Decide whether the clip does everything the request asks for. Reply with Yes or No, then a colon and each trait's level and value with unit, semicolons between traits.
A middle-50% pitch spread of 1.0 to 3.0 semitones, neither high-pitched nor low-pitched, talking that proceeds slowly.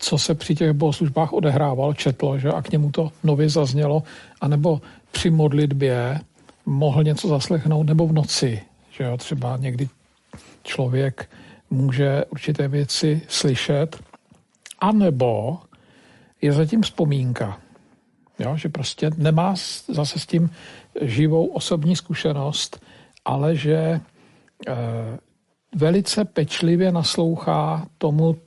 Yes: narrow, 2.6 semitones; medium, 155 Hz; slow, 110 wpm